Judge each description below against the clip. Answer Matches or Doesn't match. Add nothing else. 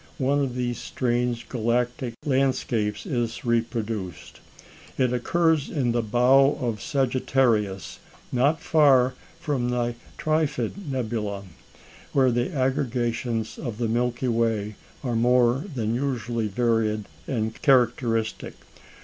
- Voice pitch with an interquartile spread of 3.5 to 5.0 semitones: Doesn't match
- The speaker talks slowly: Matches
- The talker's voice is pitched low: Matches